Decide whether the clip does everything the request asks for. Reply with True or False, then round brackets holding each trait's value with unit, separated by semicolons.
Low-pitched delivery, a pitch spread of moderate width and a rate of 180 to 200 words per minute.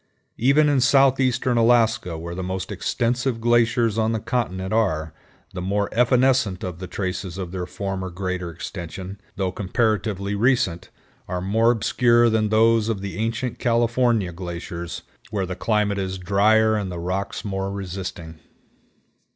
False (100 Hz; 4.0 semitones; 145 wpm)